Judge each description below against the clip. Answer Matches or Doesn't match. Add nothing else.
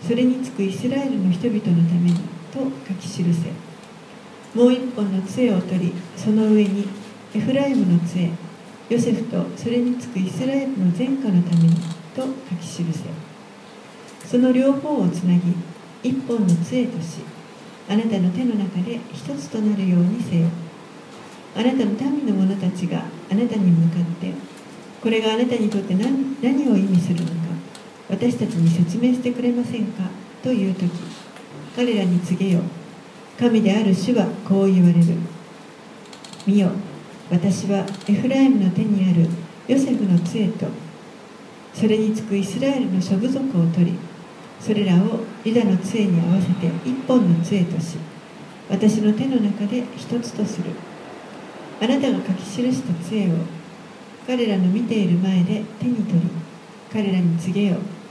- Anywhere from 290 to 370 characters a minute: Doesn't match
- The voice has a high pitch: Matches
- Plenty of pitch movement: Doesn't match